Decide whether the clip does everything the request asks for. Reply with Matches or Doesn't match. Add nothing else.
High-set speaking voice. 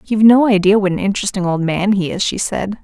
Matches